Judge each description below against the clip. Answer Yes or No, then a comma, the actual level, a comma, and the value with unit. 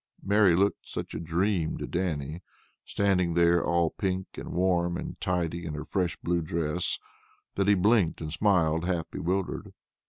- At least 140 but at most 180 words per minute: Yes, average, 160 wpm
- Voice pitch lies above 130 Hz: No, very low, 85 Hz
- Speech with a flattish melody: Yes, narrow, 2.3 semitones